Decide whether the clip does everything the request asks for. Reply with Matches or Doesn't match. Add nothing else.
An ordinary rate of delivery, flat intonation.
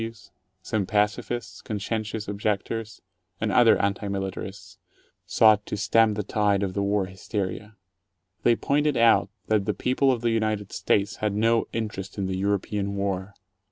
Matches